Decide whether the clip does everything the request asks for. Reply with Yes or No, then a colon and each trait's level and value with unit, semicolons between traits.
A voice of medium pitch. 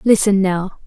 No: high, 195 Hz